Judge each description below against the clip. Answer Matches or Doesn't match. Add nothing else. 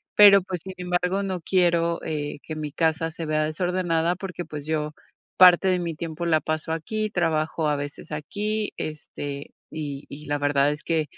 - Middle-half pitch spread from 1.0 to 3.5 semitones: Matches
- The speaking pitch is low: Doesn't match